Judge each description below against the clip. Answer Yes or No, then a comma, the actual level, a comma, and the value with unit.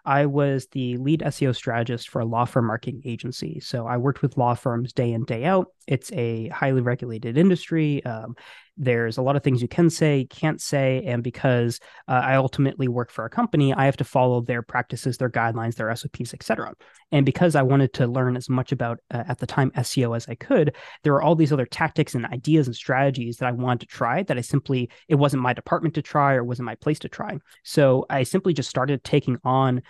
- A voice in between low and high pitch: No, low, 130 Hz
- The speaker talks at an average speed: No, fast, 225 wpm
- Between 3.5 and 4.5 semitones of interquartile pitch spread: No, average, 2.7 semitones